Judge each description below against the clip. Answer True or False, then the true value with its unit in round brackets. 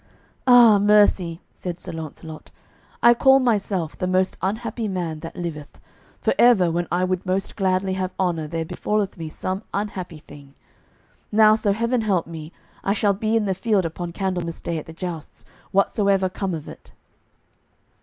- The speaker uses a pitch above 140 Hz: True (185 Hz)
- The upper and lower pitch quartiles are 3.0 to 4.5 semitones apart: True (3.7 semitones)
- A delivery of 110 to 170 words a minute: True (165 wpm)